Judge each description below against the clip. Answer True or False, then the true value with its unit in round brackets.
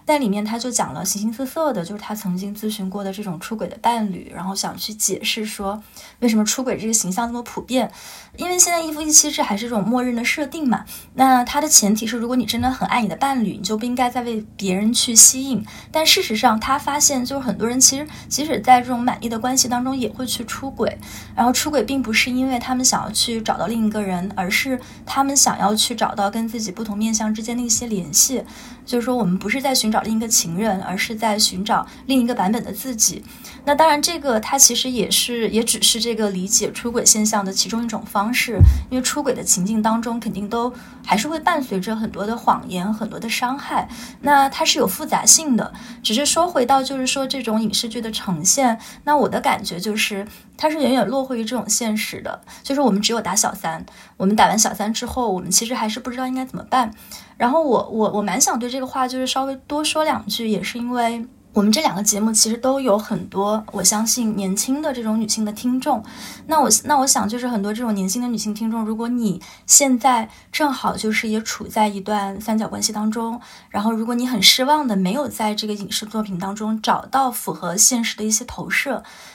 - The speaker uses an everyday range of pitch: True (3.3 semitones)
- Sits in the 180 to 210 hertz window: False (230 Hz)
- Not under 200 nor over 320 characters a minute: False (335 characters per minute)